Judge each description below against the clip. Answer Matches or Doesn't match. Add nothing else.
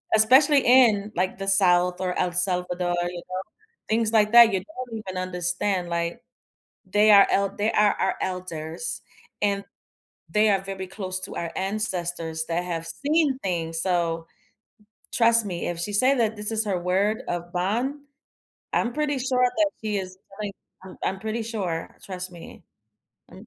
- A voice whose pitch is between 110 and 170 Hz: Doesn't match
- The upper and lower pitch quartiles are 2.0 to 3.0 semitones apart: Doesn't match